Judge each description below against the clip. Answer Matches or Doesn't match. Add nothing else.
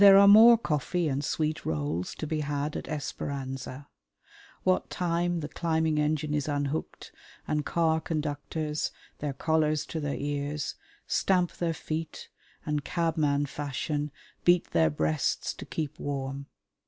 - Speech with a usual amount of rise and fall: Doesn't match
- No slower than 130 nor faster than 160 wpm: Matches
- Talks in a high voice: Doesn't match